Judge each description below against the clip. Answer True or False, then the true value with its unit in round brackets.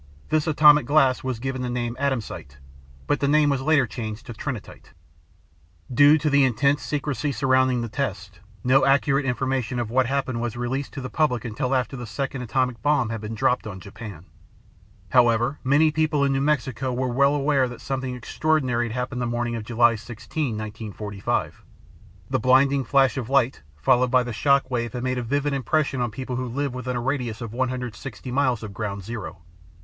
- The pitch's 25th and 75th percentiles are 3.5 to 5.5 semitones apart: False (2.8 semitones)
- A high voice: False (130 Hz)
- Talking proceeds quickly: False (190 wpm)